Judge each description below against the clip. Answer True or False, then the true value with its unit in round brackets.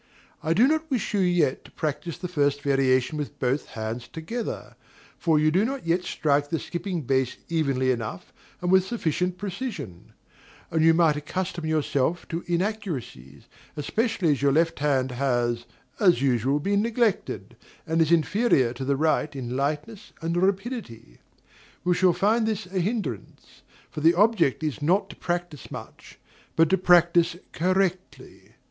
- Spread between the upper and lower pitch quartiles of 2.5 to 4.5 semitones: False (5.2 semitones)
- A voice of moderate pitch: True (165 Hz)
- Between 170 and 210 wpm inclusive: False (155 wpm)